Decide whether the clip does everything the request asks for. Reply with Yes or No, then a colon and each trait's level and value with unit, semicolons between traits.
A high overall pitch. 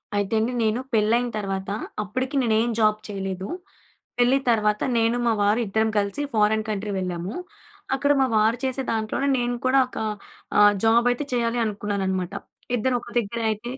Yes: high, 220 Hz